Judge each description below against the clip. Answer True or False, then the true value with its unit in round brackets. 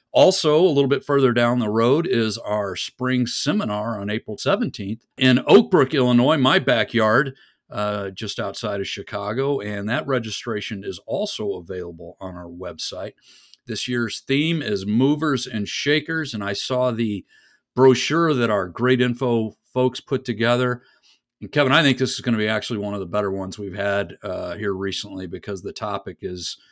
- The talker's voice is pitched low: True (115 Hz)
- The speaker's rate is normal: True (175 wpm)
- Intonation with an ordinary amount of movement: True (4.5 semitones)